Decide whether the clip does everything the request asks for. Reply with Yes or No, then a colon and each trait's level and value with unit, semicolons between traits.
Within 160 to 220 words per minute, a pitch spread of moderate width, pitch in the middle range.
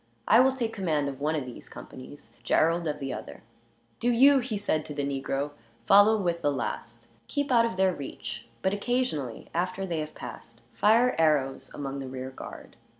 No: average, 190 wpm; wide, 7.7 semitones; medium, 165 Hz